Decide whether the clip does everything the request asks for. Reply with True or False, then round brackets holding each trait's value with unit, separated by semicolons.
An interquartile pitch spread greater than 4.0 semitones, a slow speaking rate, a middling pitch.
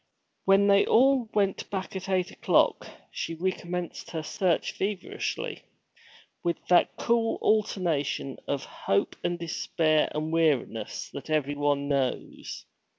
True (4.8 semitones; 120 wpm; 170 Hz)